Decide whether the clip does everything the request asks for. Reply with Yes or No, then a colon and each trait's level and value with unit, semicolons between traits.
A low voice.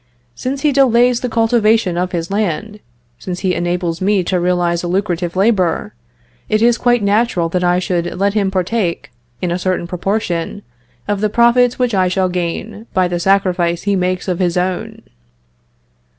No: medium, 185 Hz